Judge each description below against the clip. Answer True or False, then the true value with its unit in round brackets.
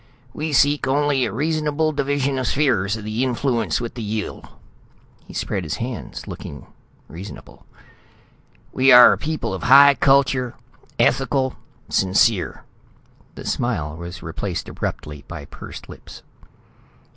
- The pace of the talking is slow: True (125 wpm)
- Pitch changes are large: True (6.2 semitones)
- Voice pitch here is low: True (125 Hz)